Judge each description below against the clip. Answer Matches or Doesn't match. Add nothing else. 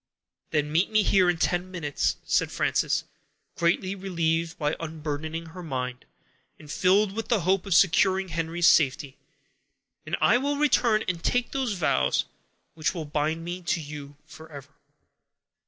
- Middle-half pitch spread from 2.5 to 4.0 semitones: Matches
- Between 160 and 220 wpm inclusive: Doesn't match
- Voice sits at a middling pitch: Matches